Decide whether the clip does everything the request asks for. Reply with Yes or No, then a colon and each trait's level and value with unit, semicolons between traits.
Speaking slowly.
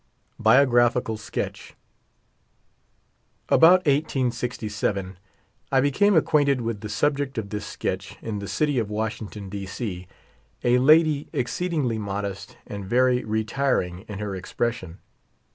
Yes: slow, 120 wpm